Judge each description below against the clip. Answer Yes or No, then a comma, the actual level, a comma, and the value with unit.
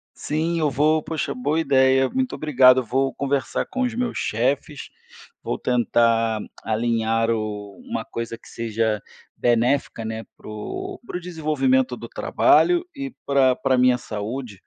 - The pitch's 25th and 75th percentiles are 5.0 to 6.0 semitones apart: Yes, wide, 5.4 semitones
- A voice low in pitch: Yes, low, 130 Hz